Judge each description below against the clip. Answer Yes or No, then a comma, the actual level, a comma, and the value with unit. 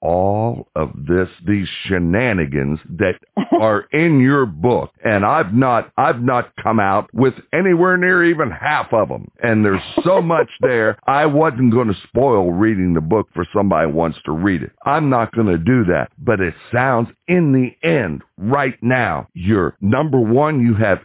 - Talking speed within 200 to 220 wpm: No, average, 180 wpm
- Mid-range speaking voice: No, low, 115 Hz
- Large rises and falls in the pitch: Yes, wide, 6.1 semitones